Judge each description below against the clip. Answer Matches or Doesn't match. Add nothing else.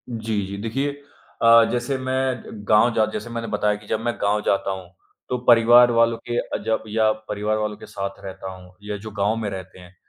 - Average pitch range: Doesn't match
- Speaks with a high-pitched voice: Doesn't match